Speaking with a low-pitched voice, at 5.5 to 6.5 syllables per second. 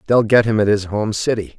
Yes: low, 105 Hz; 5.7 syllables/s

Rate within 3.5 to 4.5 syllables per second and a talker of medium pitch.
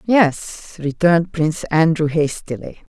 Yes: 4.0 syllables/s; medium, 160 Hz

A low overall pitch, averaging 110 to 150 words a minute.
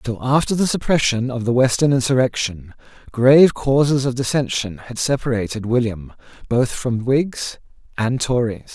Yes: low, 125 Hz; slow, 135 wpm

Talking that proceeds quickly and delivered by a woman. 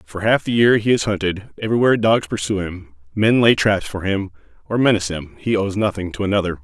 No: fast, 215 wpm; male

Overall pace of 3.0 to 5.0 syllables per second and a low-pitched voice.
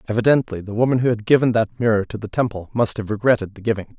No: 6.9 syllables/s; low, 110 Hz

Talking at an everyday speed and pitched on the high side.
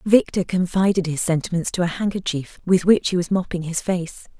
No: average, 190 wpm; medium, 180 Hz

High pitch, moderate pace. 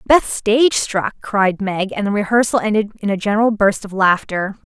Yes: high, 210 Hz; average, 190 wpm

